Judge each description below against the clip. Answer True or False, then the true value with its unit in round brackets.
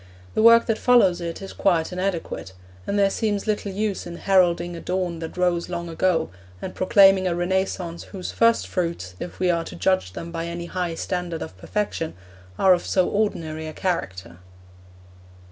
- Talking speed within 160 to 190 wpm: True (180 wpm)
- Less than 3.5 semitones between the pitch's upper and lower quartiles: True (2.5 semitones)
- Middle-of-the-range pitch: True (180 Hz)